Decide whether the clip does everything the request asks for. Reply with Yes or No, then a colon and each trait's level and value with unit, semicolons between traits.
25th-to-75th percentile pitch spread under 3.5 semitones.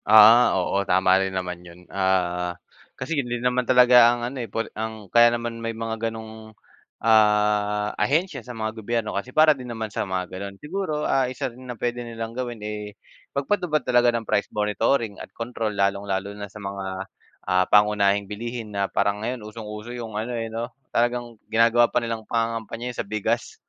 Yes: average, 2.8 semitones